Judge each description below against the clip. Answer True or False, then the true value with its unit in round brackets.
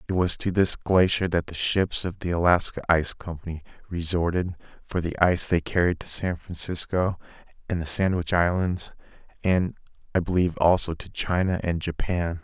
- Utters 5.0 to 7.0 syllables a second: True (5.2 syllables/s)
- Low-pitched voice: True (85 Hz)